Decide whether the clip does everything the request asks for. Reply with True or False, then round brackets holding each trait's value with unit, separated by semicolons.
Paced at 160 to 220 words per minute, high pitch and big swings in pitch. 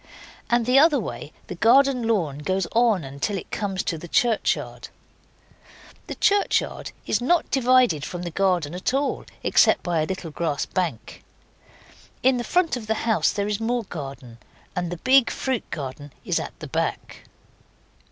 True (165 wpm; 200 Hz; 7.0 semitones)